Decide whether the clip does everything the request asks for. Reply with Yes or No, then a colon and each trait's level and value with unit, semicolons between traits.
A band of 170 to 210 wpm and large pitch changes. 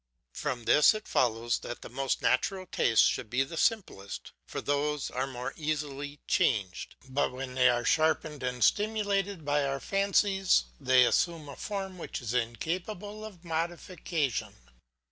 No: average, 150 wpm; wide, 6.3 semitones